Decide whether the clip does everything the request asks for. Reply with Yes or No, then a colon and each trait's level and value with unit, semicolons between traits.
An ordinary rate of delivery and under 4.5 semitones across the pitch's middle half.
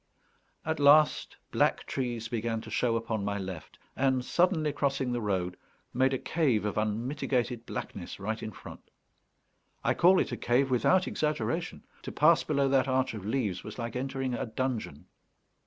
Yes: average, 165 wpm; average, 4.0 semitones